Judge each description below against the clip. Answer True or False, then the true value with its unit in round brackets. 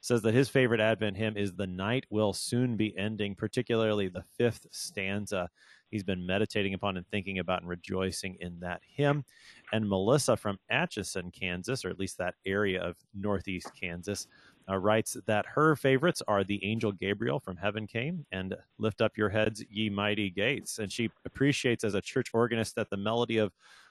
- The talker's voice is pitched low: True (105 Hz)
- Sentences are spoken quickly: False (185 wpm)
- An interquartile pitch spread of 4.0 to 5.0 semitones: False (3.0 semitones)